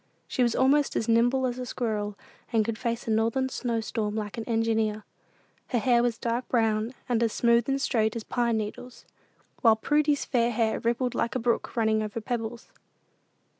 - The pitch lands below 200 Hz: No, high, 230 Hz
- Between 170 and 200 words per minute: Yes, average, 185 wpm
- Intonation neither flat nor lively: No, narrow, 1.9 semitones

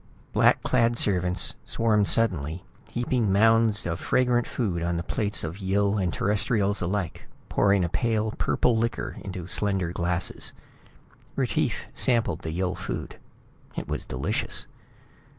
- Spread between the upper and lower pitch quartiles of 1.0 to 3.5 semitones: No, average, 4.1 semitones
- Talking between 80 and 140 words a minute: Yes, slow, 135 wpm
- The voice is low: Yes, low, 100 Hz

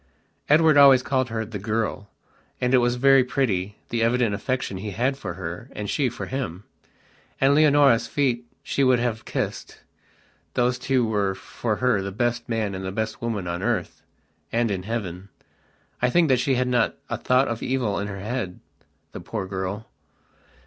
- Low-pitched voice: Yes, low, 115 Hz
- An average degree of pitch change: Yes, average, 4.0 semitones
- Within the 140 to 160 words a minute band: No, average, 170 wpm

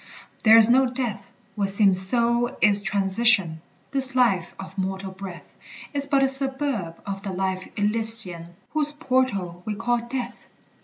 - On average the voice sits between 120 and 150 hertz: No, high, 210 Hz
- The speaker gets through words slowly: No, average, 150 wpm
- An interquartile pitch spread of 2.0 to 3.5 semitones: No, average, 4.7 semitones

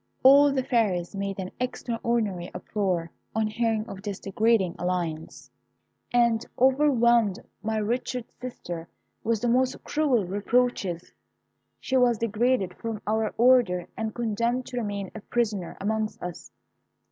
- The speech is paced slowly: Yes, slow, 130 wpm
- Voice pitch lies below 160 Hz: No, high, 220 Hz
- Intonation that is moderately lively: Yes, average, 3.8 semitones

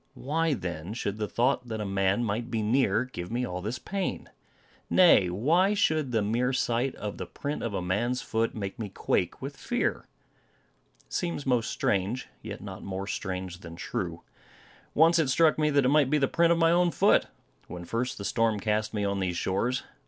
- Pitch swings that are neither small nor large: No, wide, 6.0 semitones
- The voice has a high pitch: No, low, 115 Hz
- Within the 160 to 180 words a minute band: No, average, 200 wpm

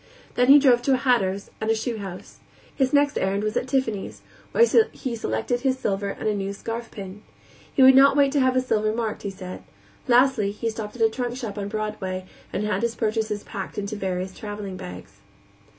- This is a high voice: Yes, high, 220 Hz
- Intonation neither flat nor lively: Yes, average, 4.0 semitones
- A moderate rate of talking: No, fast, 210 wpm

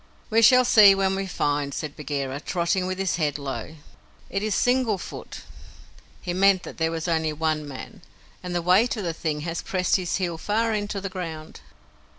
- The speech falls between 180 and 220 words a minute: Yes, average, 190 wpm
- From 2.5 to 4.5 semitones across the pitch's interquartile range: Yes, average, 3.9 semitones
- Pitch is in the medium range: Yes, medium, 180 Hz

